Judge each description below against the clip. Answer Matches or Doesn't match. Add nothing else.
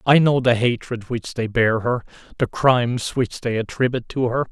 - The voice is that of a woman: Doesn't match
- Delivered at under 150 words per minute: Doesn't match